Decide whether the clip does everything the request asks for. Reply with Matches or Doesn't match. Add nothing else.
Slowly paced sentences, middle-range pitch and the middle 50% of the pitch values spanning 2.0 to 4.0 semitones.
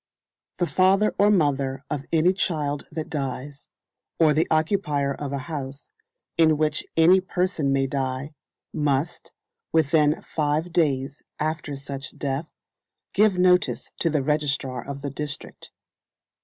Matches